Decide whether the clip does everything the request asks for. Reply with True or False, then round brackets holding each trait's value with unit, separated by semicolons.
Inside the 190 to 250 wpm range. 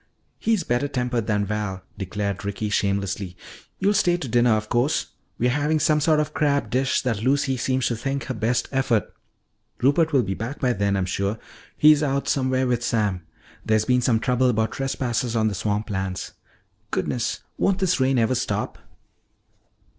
False (175 wpm)